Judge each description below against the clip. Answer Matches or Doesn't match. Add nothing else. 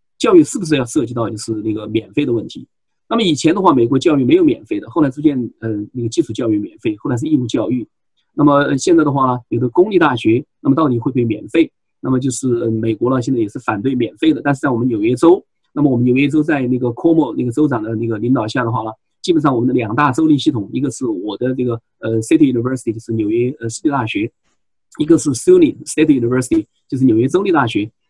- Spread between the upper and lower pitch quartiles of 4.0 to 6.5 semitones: Matches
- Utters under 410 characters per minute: Doesn't match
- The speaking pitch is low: Matches